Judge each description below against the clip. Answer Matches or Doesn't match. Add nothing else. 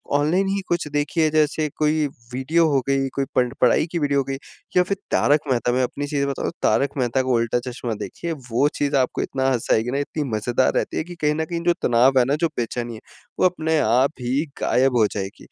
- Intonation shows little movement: Doesn't match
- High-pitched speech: Doesn't match